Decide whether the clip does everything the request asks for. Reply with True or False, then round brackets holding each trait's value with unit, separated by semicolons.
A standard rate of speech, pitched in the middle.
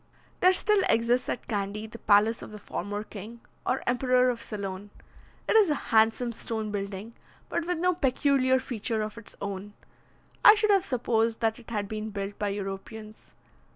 False (175 wpm; 225 Hz)